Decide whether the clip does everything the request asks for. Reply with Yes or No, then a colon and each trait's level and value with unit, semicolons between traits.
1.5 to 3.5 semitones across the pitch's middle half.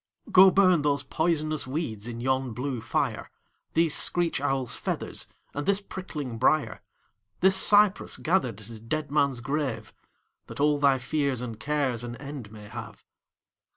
No: average, 4.4 semitones